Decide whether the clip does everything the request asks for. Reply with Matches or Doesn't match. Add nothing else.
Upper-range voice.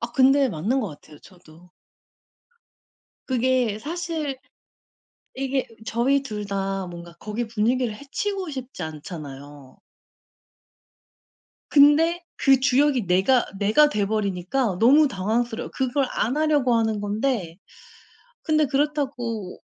Matches